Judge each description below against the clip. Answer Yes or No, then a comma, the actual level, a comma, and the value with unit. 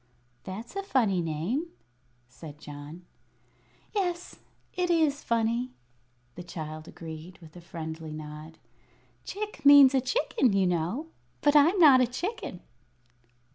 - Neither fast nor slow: No, slow, 125 wpm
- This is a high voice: Yes, high, 210 Hz